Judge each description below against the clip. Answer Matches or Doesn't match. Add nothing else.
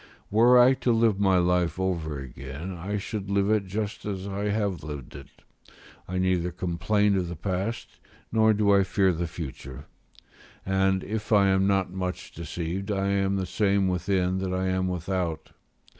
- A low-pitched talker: Matches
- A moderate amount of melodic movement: Doesn't match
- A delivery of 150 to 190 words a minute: Matches